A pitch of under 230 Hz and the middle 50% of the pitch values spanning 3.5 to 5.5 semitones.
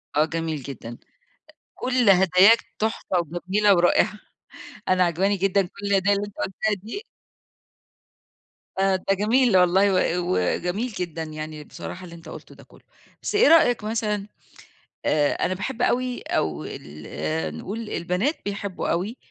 Yes: high, 190 Hz; average, 4.0 semitones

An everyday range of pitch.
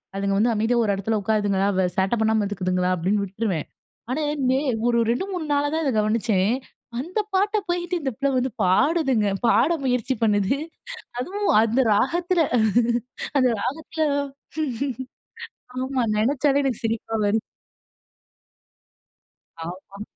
No: wide, 5.7 semitones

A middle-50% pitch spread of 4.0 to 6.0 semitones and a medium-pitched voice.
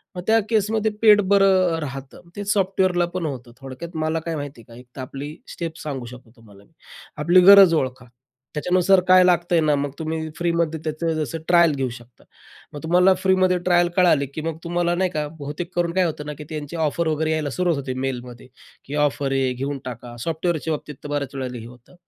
Yes: average, 4.4 semitones; medium, 160 Hz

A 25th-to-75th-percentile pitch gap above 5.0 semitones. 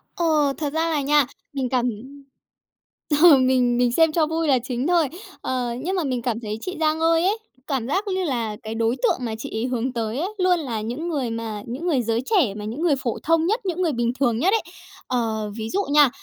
Yes: wide, 5.6 semitones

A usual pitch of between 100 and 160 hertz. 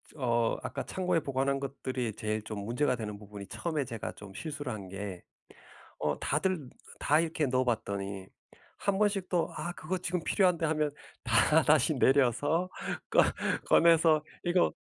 Yes: medium, 140 Hz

